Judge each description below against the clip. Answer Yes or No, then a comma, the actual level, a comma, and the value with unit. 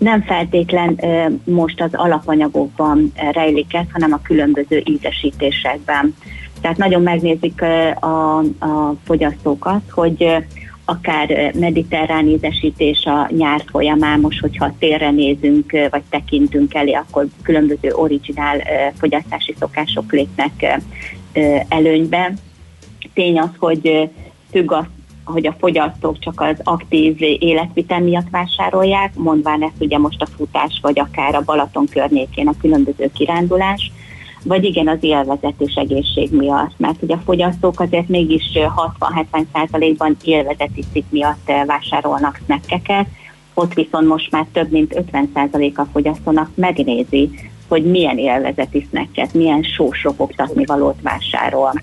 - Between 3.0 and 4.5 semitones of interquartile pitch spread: No, narrow, 2.5 semitones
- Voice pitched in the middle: Yes, medium, 155 Hz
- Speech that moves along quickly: No, average, 120 wpm